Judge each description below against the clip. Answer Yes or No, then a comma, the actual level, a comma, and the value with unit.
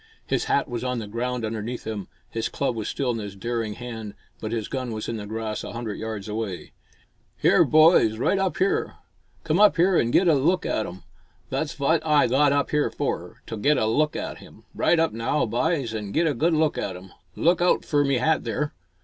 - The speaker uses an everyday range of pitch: No, wide, 5.7 semitones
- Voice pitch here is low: Yes, low, 125 Hz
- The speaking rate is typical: No, fast, 225 wpm